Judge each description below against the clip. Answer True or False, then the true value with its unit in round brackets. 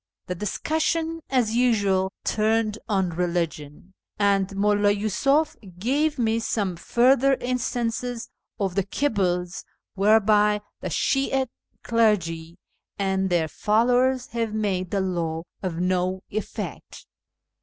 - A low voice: False (210 Hz)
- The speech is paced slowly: True (110 wpm)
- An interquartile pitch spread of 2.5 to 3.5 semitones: False (4.4 semitones)